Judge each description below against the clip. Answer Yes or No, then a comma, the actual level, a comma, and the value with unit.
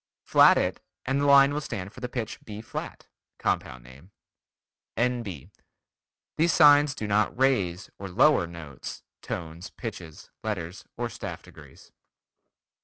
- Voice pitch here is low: Yes, low, 105 Hz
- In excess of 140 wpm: No, slow, 135 wpm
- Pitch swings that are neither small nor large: No, wide, 7.3 semitones